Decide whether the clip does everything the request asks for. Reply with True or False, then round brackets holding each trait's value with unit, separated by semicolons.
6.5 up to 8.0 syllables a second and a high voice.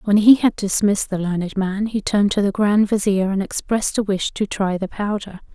False (5.5 syllables/s; 200 Hz)